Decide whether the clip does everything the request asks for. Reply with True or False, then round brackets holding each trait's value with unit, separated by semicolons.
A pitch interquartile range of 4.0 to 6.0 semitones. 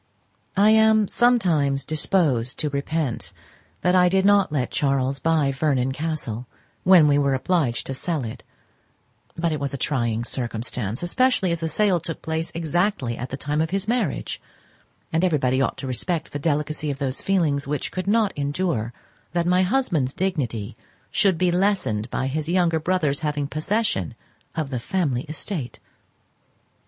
True (5.3 semitones)